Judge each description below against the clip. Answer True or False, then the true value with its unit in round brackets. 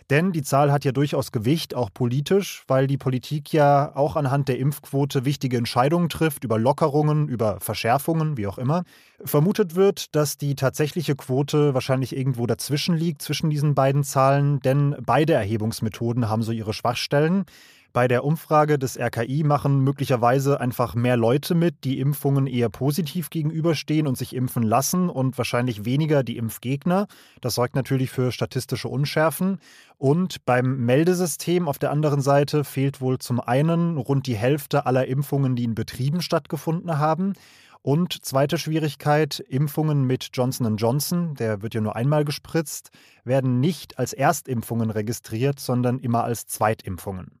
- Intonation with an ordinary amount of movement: True (3.5 semitones)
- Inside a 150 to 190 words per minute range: True (155 wpm)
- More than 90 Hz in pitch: True (140 Hz)